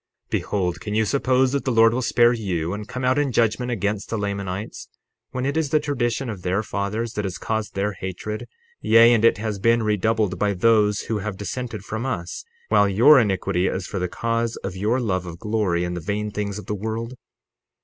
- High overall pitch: No, low, 105 Hz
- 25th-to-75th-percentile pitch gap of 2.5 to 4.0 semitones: Yes, average, 3.0 semitones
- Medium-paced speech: No, fast, 215 wpm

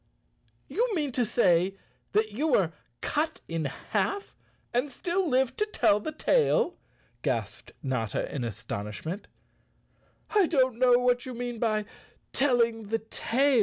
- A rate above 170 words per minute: No, slow, 135 wpm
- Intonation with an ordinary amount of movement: No, wide, 6.2 semitones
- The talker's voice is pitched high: Yes, high, 245 Hz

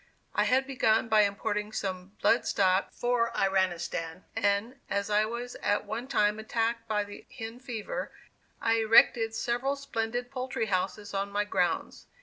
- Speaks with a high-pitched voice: Yes, high, 220 Hz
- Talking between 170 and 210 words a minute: No, average, 150 wpm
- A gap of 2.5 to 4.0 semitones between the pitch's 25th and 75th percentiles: Yes, average, 2.9 semitones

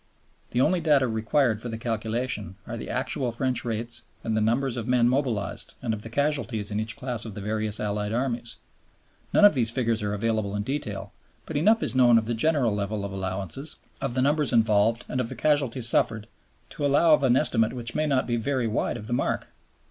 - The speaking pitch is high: No, low, 115 Hz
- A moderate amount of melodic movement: Yes, average, 3.3 semitones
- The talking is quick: Yes, fast, 215 wpm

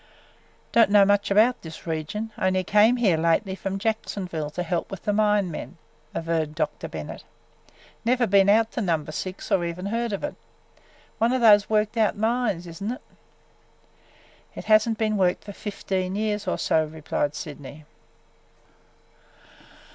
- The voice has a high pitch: Yes, high, 200 Hz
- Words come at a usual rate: Yes, average, 160 wpm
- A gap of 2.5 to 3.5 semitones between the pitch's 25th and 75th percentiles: No, average, 4.3 semitones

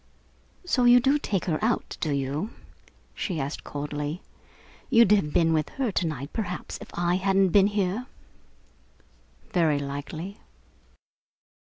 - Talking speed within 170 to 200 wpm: No, slow, 135 wpm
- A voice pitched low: No, medium, 180 Hz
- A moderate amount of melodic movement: No, wide, 5.9 semitones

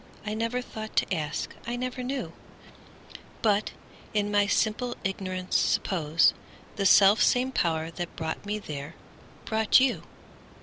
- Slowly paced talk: Yes, slow, 125 wpm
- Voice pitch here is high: Yes, high, 205 Hz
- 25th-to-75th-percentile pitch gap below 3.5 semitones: No, average, 4.7 semitones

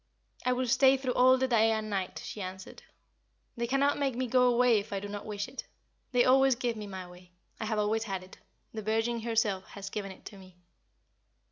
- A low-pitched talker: No, high, 225 Hz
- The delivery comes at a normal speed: No, fast, 220 wpm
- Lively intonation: No, average, 3.8 semitones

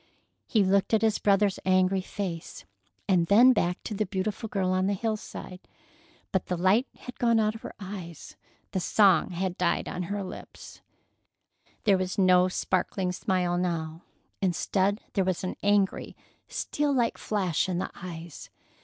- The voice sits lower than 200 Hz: Yes, high, 190 Hz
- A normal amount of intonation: No, narrow, 2.2 semitones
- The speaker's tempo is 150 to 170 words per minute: Yes, average, 160 wpm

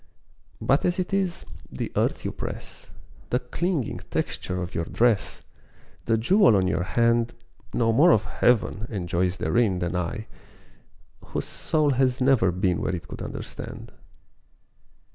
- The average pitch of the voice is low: Yes, low, 115 Hz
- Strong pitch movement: Yes, wide, 6.5 semitones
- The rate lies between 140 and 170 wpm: Yes, average, 145 wpm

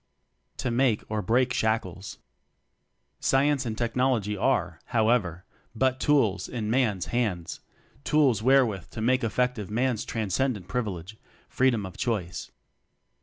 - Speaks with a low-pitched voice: Yes, low, 115 Hz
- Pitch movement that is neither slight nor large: Yes, average, 3.7 semitones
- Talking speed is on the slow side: Yes, slow, 120 wpm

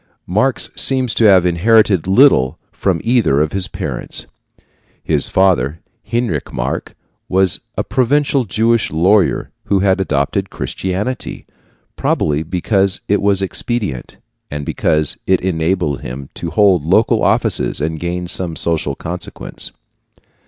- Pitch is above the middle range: No, very low, 95 Hz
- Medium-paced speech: No, slow, 125 wpm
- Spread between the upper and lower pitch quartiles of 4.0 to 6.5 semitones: Yes, average, 4.7 semitones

